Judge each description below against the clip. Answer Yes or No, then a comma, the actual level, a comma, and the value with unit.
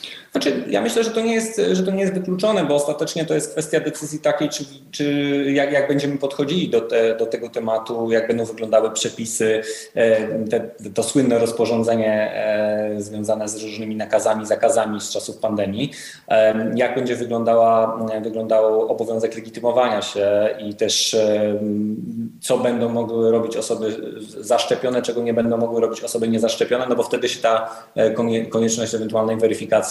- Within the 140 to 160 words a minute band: Yes, average, 155 wpm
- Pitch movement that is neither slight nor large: Yes, average, 4.0 semitones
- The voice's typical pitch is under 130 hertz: Yes, low, 115 Hz